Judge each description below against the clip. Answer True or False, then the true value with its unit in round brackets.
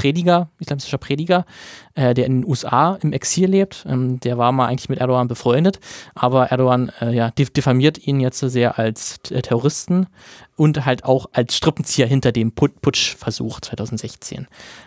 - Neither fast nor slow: True (145 wpm)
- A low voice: True (130 Hz)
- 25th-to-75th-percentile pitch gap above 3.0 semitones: True (3.5 semitones)